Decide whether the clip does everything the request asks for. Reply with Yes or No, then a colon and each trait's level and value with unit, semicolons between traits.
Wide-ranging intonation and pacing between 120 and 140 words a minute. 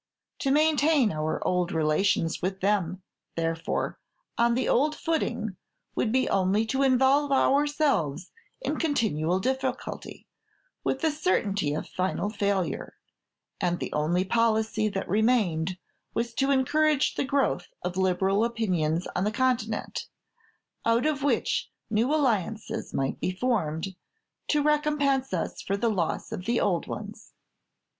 Yes: wide, 6.5 semitones; slow, 135 wpm